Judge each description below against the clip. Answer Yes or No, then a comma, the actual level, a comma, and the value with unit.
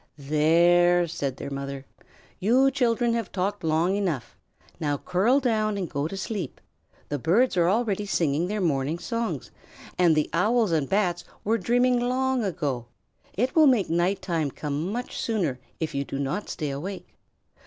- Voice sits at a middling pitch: Yes, medium, 180 Hz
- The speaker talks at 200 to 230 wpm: No, average, 165 wpm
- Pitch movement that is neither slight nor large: No, wide, 6.5 semitones